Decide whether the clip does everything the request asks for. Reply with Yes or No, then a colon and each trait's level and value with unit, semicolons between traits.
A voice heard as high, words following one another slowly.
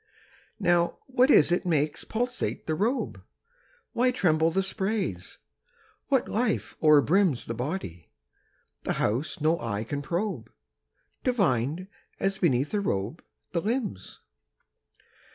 No: medium, 170 Hz; slow, 120 wpm